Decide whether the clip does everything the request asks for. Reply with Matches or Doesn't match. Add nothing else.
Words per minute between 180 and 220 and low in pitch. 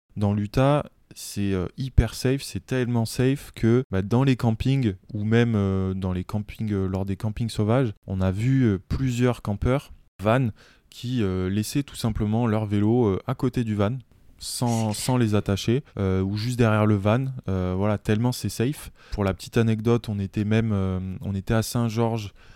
Matches